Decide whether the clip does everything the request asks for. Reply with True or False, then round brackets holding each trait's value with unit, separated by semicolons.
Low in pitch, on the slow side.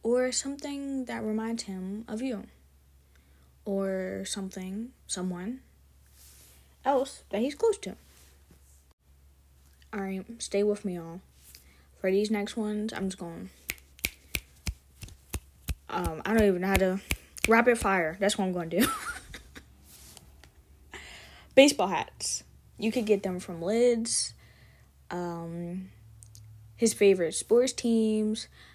False (180 Hz; 115 wpm)